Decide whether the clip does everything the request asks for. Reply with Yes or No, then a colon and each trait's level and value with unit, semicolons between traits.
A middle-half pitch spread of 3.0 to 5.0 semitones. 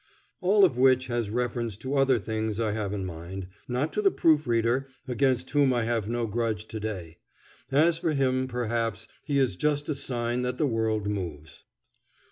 Yes: average, 3.7 semitones